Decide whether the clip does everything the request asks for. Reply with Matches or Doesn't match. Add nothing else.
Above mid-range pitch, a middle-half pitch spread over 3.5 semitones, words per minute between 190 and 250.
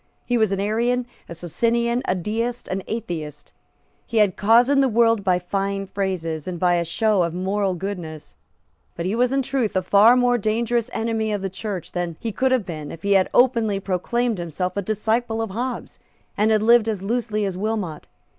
Matches